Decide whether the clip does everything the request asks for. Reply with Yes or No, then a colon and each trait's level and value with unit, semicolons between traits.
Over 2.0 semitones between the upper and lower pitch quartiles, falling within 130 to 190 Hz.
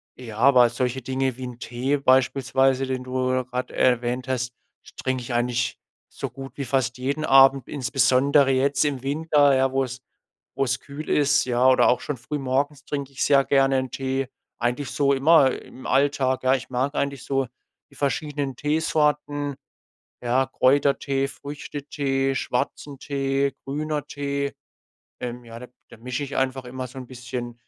No: narrow, 1.7 semitones; low, 135 Hz